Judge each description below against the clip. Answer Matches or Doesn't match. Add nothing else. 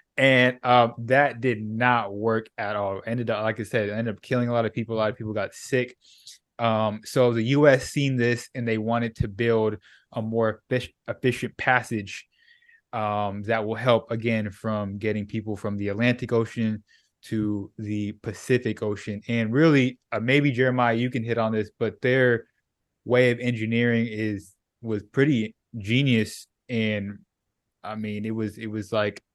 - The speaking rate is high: Doesn't match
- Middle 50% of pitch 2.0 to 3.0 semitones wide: Matches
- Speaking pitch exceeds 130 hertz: Doesn't match